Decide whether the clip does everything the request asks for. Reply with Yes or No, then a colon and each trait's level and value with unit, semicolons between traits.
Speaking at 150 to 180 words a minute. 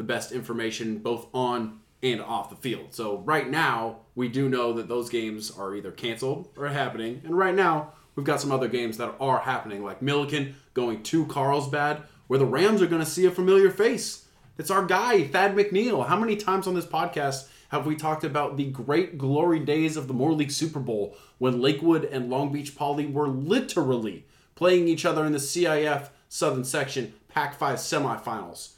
No: average, 195 wpm